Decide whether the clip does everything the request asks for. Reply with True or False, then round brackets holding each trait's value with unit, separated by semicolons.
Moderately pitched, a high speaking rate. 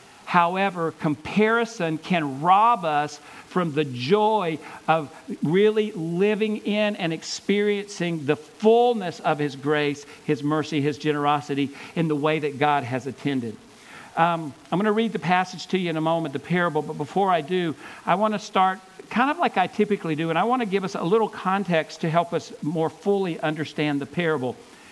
False (170 Hz; 180 wpm)